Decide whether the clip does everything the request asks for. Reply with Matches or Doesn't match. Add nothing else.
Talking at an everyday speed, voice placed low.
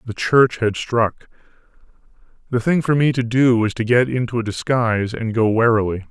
Matches